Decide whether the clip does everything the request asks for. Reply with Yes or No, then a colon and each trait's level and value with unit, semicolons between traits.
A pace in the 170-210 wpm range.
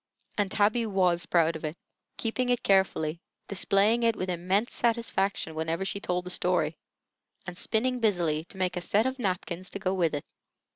Yes: average, 180 wpm